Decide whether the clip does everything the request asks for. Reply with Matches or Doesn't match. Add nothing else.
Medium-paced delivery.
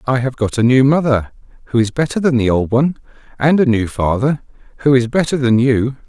Doesn't match